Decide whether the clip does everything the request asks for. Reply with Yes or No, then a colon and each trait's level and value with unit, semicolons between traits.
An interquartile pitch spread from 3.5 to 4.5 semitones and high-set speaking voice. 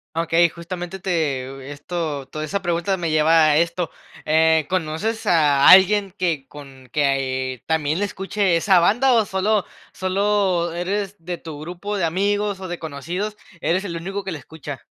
No: average, 3.9 semitones; medium, 170 Hz